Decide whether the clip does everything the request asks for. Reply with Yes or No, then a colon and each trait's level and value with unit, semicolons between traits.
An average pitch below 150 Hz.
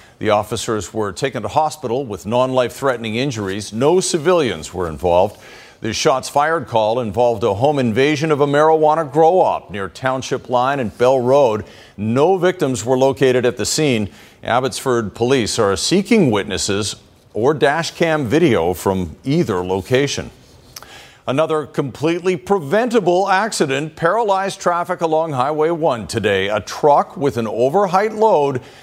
Yes: low, 135 Hz